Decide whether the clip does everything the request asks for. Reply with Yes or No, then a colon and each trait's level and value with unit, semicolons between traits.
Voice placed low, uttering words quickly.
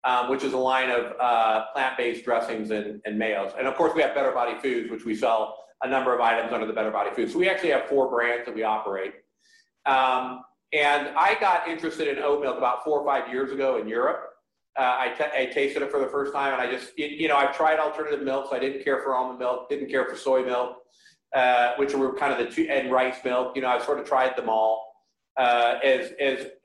Yes: low, 130 Hz; fast, 245 wpm